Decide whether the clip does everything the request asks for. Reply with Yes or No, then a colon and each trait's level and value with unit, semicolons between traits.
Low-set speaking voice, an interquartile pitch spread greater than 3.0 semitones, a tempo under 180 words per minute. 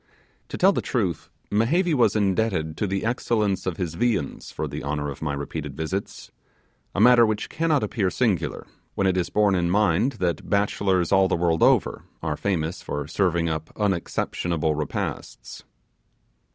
Yes: very low, 95 Hz; average, 4.7 semitones; average, 165 wpm